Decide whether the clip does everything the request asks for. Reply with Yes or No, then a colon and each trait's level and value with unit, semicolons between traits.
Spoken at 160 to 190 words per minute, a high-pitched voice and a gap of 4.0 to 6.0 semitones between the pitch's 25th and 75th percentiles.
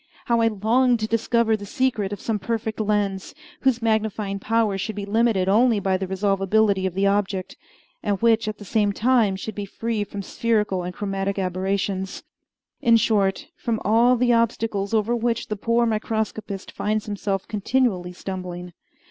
No: average, 165 wpm; high, 210 Hz; average, 2.7 semitones